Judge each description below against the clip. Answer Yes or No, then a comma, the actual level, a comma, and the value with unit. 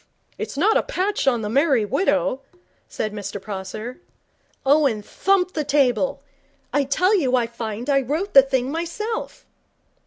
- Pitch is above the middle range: Yes, very high, 275 Hz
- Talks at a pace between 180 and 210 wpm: No, average, 150 wpm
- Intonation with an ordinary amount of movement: No, wide, 6.3 semitones